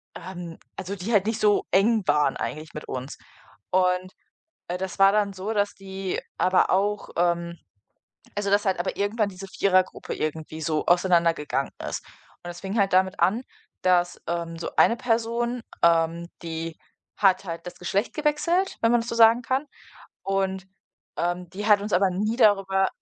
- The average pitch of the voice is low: No, high, 190 Hz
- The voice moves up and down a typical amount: Yes, average, 3.1 semitones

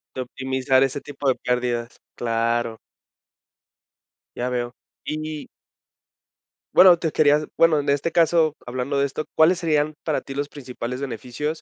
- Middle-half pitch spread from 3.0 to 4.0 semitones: Yes, average, 3.7 semitones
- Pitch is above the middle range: No, medium, 140 Hz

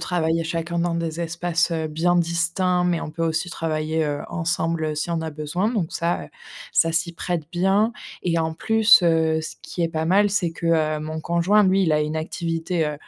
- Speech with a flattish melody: Yes, narrow, 1.6 semitones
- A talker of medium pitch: Yes, medium, 165 Hz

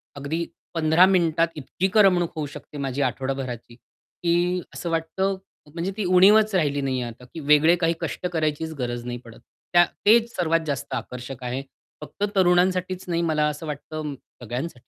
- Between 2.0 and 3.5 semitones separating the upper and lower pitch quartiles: No, average, 4.3 semitones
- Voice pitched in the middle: Yes, medium, 160 Hz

